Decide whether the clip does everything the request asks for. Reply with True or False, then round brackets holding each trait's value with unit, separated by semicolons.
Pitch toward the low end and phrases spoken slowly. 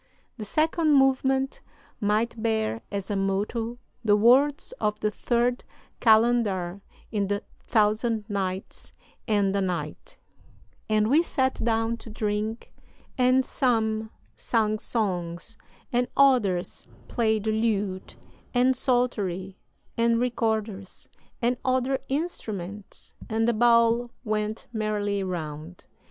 False (220 Hz; 115 wpm)